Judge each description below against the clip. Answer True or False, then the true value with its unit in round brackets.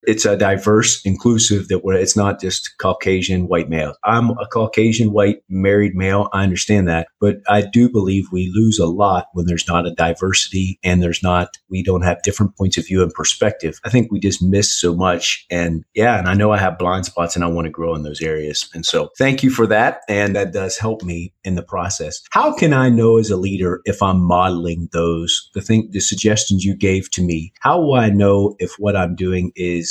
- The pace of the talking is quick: True (225 wpm)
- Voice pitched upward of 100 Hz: False (95 Hz)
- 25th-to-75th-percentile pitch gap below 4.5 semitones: True (2.7 semitones)